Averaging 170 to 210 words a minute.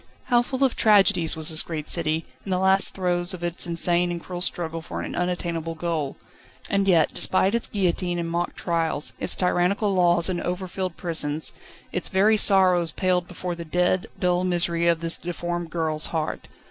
Yes: average, 180 wpm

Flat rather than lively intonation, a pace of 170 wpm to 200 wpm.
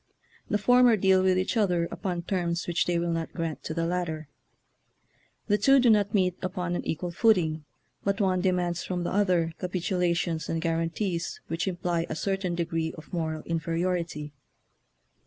Yes: narrow, 2.3 semitones; average, 175 wpm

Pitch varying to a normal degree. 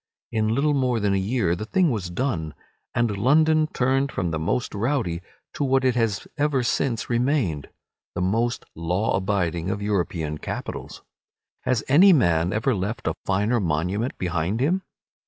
No: wide, 6.5 semitones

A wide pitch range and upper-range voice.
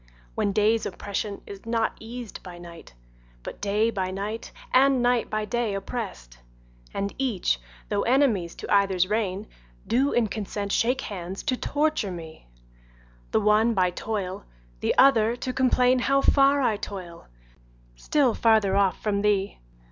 No: average, 3.8 semitones; high, 210 Hz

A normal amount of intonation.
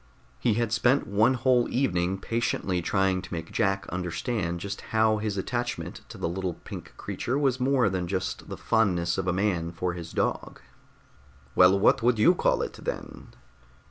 Yes: average, 4.6 semitones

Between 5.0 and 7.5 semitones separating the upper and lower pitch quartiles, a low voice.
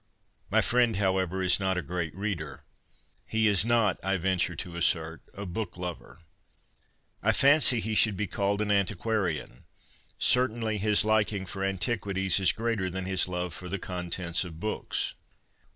No: average, 3.1 semitones; very low, 95 Hz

